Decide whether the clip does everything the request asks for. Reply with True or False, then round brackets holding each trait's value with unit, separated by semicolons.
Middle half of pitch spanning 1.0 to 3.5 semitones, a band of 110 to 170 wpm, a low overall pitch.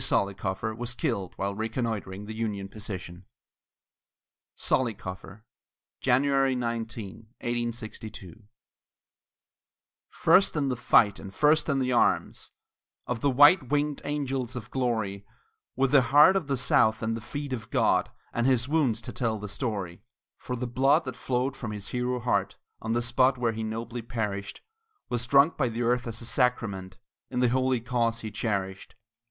True (3.1 semitones; 155 wpm; 120 Hz)